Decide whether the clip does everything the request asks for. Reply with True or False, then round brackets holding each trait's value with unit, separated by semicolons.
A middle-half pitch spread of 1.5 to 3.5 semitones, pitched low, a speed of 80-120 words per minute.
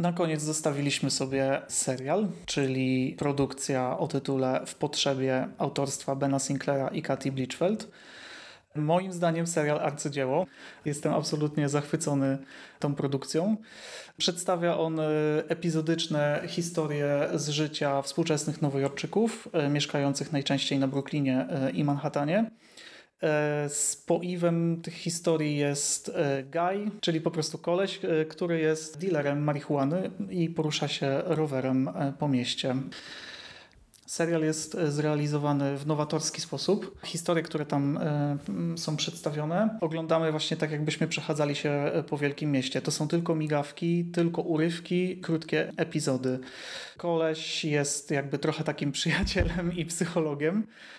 False (2.7 semitones; 155 Hz; 110 wpm)